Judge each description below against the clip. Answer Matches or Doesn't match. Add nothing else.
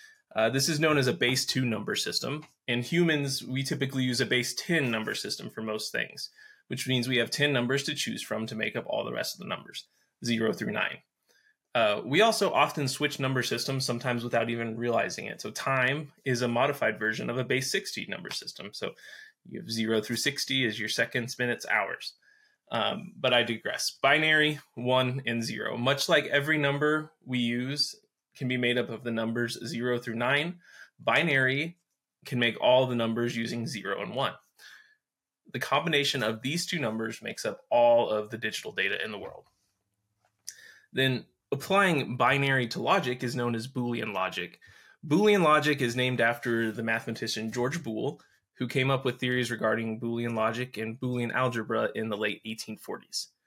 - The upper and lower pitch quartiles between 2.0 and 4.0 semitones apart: Matches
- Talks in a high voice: Doesn't match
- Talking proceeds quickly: Doesn't match